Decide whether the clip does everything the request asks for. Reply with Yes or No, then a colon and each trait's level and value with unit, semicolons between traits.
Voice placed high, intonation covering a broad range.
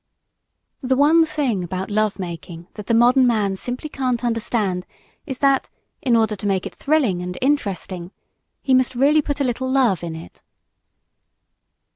Yes: high, 235 Hz; wide, 5.7 semitones